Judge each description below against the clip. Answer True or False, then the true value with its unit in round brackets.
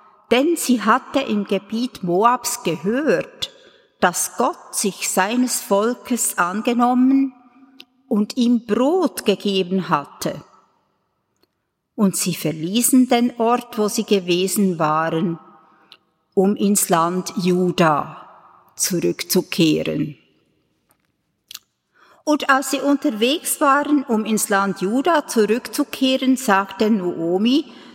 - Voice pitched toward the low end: False (220 Hz)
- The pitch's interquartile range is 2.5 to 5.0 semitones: False (5.5 semitones)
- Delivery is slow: True (95 wpm)